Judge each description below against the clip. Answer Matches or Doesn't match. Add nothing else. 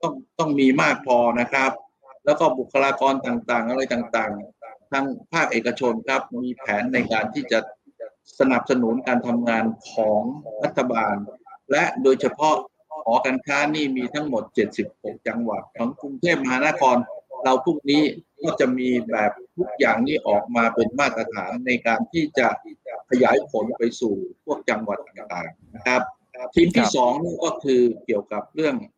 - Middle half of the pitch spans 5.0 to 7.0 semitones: Doesn't match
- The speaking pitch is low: Matches